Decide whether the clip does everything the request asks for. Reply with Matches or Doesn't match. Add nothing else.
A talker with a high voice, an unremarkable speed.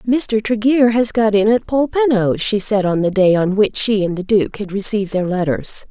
Doesn't match